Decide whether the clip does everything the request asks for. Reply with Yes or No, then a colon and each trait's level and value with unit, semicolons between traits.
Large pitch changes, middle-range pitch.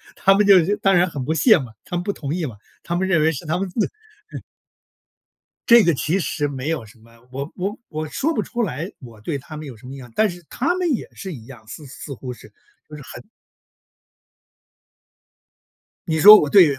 Yes: wide, 6.2 semitones; medium, 160 Hz